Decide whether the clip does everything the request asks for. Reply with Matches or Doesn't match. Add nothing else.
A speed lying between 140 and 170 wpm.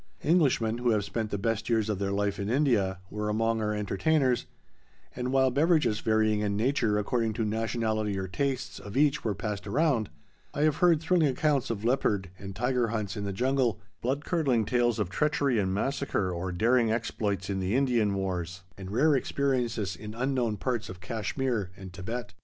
Doesn't match